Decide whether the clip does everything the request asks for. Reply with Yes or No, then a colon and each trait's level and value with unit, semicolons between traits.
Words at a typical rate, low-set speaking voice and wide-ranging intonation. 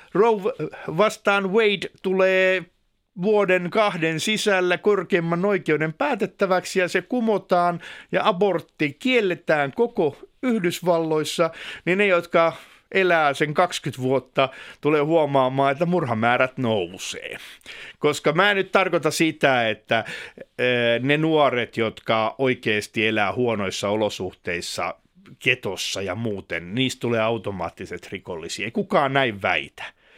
No: average, 110 wpm; medium, 165 Hz; wide, 6.4 semitones